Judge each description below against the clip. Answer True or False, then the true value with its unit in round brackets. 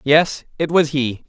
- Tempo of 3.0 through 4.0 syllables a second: True (3.8 syllables/s)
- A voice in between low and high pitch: True (145 Hz)